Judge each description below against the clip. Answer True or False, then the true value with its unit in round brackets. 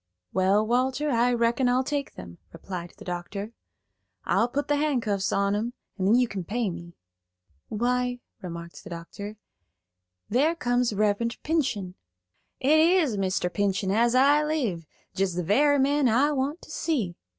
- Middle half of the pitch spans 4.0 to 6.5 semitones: True (5.5 semitones)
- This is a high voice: True (235 Hz)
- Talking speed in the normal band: True (155 wpm)